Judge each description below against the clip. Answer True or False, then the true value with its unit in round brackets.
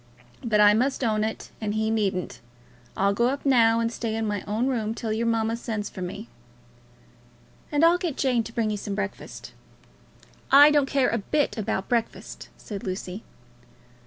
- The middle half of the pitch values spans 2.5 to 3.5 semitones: True (2.8 semitones)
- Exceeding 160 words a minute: True (180 wpm)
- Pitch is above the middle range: True (225 Hz)